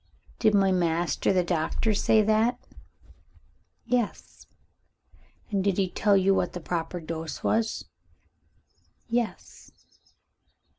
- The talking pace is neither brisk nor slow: No, slow, 105 wpm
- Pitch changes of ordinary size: Yes, average, 3.8 semitones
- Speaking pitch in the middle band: No, high, 195 Hz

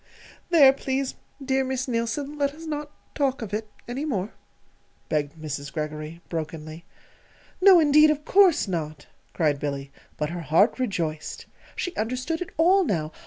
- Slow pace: No, average, 155 wpm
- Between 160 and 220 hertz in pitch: No, high, 230 Hz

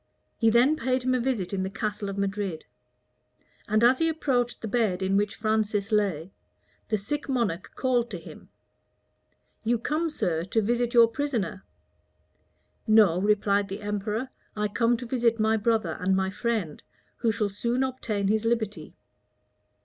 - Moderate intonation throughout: Yes, average, 3.2 semitones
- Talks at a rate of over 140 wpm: Yes, average, 160 wpm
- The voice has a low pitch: No, high, 220 Hz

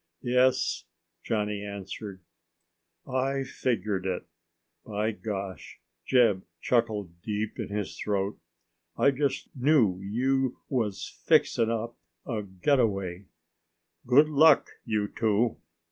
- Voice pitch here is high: No, low, 110 Hz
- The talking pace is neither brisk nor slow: No, slow, 100 wpm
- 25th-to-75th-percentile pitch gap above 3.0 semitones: Yes, average, 4.1 semitones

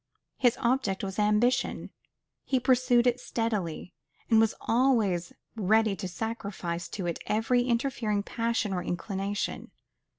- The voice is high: Yes, high, 220 Hz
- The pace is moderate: No, slow, 125 wpm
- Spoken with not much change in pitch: No, average, 3.7 semitones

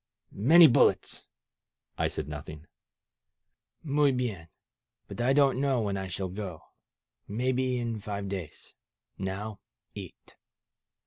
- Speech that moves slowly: Yes, slow, 115 wpm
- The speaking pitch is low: Yes, low, 110 Hz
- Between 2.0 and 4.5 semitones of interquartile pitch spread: No, average, 5.2 semitones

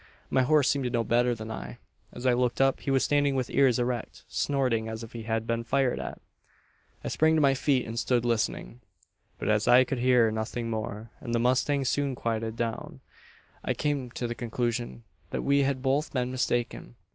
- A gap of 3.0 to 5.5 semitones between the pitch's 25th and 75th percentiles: No, narrow, 2.6 semitones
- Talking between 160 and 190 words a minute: No, fast, 205 wpm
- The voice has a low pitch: Yes, low, 120 Hz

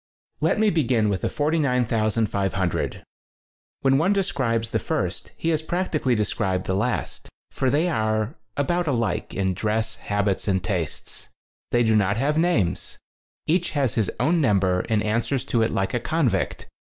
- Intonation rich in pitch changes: Yes, wide, 6.2 semitones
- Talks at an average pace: Yes, average, 160 wpm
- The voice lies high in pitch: No, low, 115 Hz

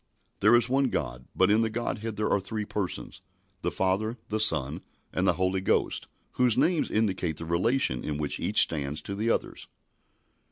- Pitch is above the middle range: No, low, 105 Hz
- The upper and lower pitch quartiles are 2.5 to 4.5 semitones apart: No, average, 5.3 semitones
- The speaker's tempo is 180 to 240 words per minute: Yes, average, 185 wpm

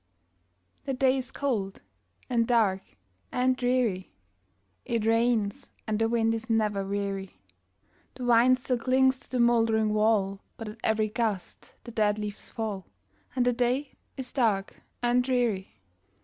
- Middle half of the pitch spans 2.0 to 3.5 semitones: Yes, average, 2.9 semitones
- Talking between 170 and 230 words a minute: No, average, 145 wpm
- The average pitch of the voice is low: No, high, 225 Hz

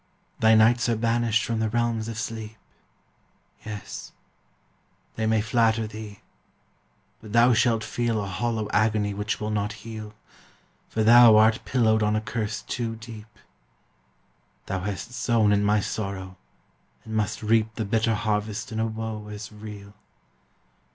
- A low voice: Yes, low, 110 Hz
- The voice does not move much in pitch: Yes, narrow, 1.3 semitones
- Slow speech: No, average, 145 wpm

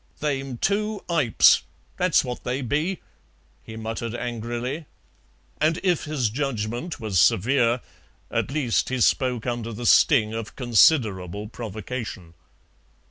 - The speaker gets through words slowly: Yes, slow, 120 wpm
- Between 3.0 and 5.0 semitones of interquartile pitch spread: Yes, average, 4.4 semitones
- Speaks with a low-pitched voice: Yes, low, 120 Hz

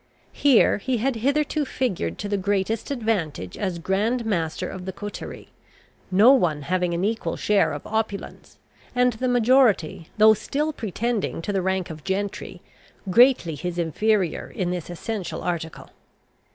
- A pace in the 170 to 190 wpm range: No, average, 150 wpm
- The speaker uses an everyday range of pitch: Yes, average, 4.8 semitones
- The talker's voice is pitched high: Yes, high, 205 Hz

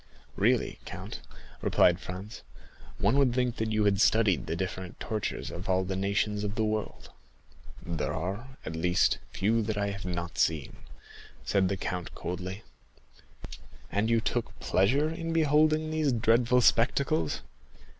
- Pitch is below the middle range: Yes, low, 105 Hz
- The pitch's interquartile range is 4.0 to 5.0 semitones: Yes, average, 4.6 semitones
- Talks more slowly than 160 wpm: Yes, average, 145 wpm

